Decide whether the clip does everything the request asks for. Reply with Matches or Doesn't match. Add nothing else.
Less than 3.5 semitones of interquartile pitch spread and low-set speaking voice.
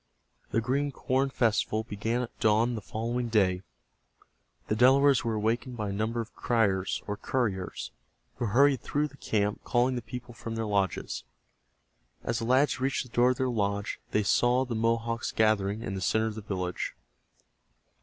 Matches